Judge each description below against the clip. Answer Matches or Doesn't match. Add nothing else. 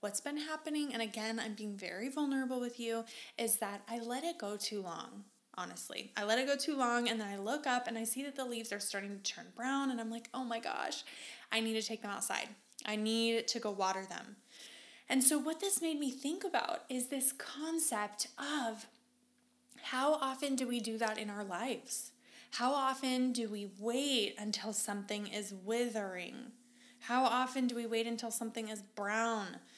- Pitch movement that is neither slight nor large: Matches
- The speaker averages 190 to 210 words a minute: Matches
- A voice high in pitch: Matches